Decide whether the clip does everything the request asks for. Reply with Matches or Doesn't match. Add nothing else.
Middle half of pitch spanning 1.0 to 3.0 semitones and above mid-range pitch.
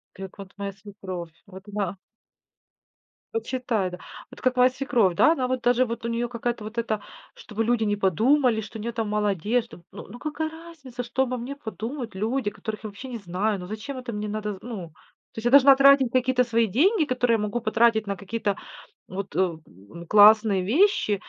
Doesn't match